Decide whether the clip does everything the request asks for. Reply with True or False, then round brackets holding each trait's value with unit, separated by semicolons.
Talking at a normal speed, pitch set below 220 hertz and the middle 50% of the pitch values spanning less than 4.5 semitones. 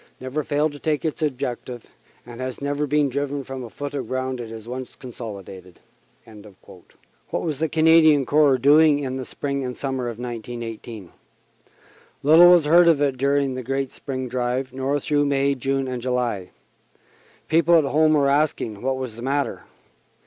True (170 wpm; 135 Hz; 2.8 semitones)